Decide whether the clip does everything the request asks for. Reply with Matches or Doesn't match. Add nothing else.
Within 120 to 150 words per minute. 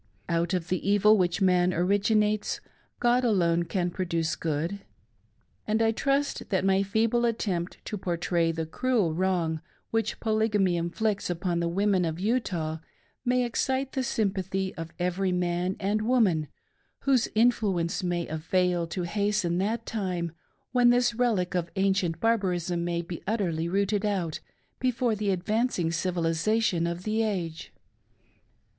Matches